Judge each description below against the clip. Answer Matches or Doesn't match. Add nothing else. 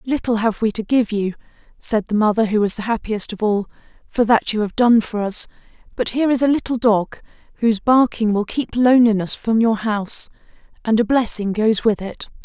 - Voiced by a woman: Matches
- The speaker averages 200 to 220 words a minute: Matches